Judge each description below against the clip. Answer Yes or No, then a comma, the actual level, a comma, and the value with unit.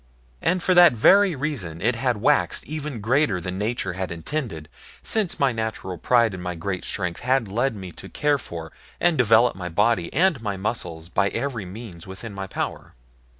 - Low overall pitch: Yes, low, 110 Hz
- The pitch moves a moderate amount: No, wide, 6.6 semitones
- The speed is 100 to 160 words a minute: No, average, 185 wpm